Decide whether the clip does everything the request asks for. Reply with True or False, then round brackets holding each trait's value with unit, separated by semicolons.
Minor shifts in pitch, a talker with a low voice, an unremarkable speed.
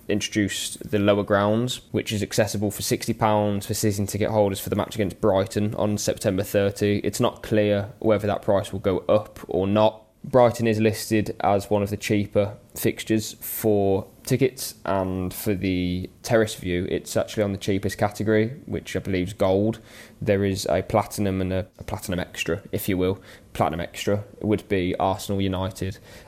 True (1.9 semitones; 105 Hz; 175 wpm)